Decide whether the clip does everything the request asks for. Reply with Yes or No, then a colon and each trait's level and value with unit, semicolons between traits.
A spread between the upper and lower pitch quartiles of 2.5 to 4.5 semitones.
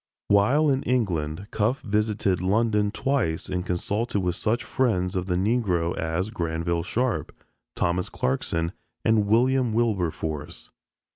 No: average, 4.9 semitones